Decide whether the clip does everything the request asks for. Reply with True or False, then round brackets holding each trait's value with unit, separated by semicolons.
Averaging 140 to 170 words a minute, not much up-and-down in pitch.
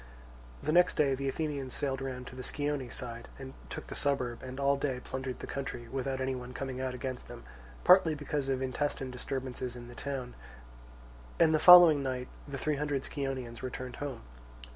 False (185 wpm; 2.0 semitones)